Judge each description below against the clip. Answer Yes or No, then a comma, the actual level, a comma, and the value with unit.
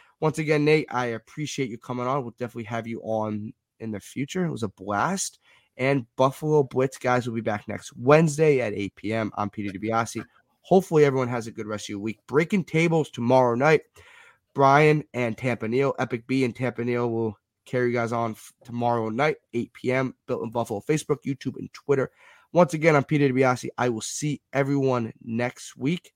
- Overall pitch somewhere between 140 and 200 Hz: No, low, 125 Hz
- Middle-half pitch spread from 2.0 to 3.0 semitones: No, average, 3.9 semitones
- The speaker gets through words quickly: No, average, 190 wpm